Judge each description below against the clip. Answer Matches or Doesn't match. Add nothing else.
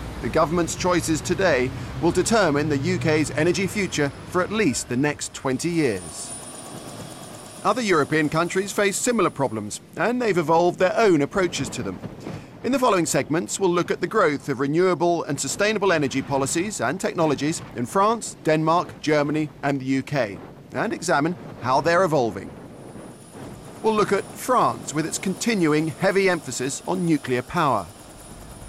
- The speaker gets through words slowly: Doesn't match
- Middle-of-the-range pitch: Matches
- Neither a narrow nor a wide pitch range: Matches